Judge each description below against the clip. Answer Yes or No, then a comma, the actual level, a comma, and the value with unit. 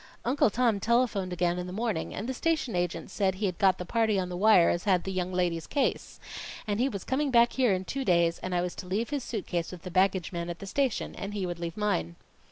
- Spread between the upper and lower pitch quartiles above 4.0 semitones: Yes, average, 4.4 semitones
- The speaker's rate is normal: No, fast, 260 wpm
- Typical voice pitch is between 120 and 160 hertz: No, high, 190 Hz